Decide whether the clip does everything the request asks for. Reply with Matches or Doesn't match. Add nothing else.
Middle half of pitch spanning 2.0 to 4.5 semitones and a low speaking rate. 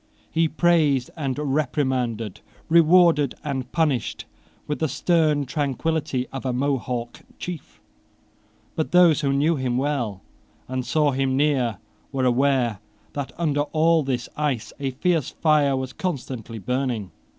Matches